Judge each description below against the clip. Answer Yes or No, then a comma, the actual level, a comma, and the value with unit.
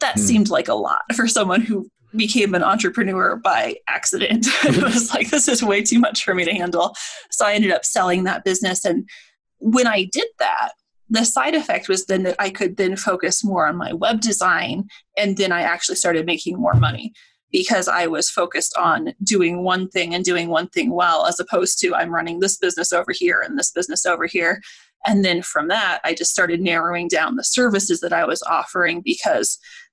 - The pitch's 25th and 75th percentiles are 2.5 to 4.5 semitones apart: No, average, 5.1 semitones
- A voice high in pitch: Yes, high, 200 Hz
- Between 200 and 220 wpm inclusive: Yes, fast, 205 wpm